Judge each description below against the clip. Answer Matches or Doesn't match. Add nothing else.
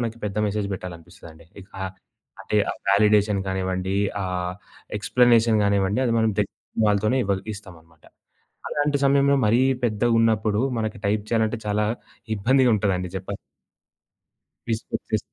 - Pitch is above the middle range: Doesn't match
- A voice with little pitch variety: Doesn't match